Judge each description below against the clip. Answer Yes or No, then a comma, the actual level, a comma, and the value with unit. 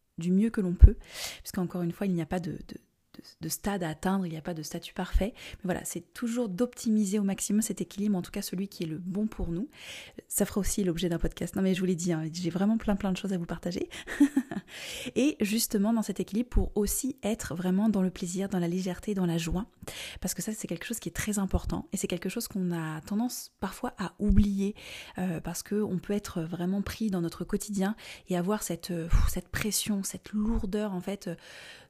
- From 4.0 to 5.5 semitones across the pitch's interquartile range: No, average, 3.1 semitones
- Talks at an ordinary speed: No, fast, 235 wpm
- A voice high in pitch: Yes, high, 195 Hz